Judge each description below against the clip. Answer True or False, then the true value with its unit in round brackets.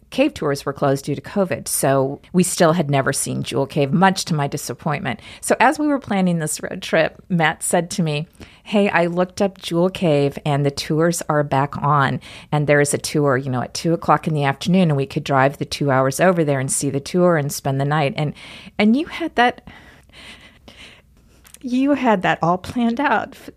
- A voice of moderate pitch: True (160 Hz)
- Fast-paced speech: True (215 wpm)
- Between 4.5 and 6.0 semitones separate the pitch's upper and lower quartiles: True (5.2 semitones)